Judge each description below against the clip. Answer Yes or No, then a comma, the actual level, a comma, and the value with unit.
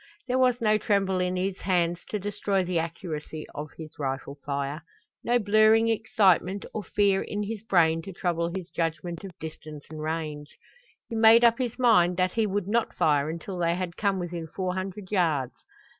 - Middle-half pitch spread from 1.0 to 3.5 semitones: No, average, 4.1 semitones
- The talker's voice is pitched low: No, medium, 180 Hz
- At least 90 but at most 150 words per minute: No, average, 185 wpm